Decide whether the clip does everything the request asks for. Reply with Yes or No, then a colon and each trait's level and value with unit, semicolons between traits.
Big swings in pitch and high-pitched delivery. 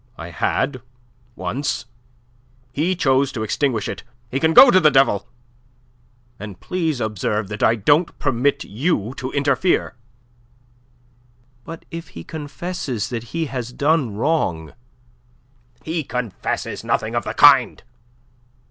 No: wide, 6.1 semitones; low, 135 Hz